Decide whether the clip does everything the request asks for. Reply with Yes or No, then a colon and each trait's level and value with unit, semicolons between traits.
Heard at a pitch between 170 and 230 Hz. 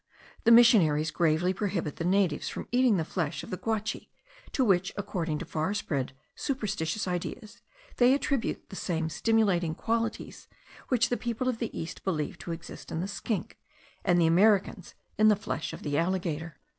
Yes: high, 190 Hz